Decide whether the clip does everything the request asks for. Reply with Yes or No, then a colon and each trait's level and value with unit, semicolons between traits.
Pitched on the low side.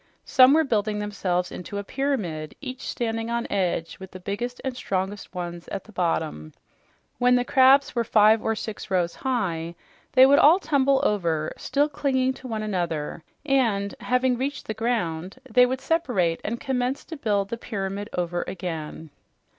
No: high, 215 Hz